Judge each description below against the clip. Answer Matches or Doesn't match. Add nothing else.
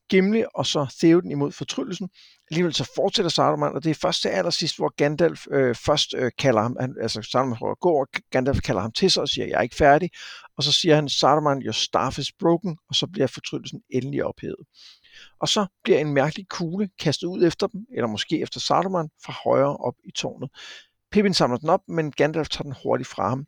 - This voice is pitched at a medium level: Matches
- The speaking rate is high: Doesn't match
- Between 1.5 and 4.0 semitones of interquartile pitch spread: Doesn't match